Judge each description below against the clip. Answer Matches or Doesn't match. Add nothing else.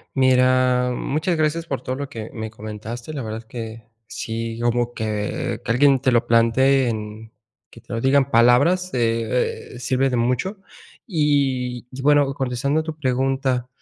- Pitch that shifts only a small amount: Doesn't match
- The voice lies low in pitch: Matches